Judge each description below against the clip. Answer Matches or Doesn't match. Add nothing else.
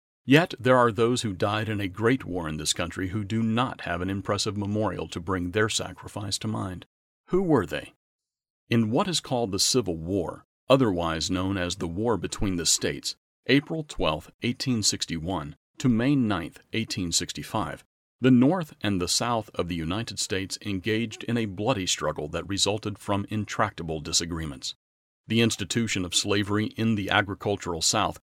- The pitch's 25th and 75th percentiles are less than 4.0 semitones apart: Doesn't match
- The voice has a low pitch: Matches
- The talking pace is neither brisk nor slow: Matches